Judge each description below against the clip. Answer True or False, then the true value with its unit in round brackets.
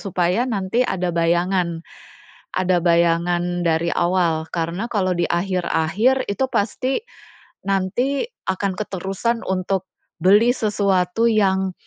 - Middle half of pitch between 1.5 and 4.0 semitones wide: True (2.9 semitones)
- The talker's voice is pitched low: False (185 Hz)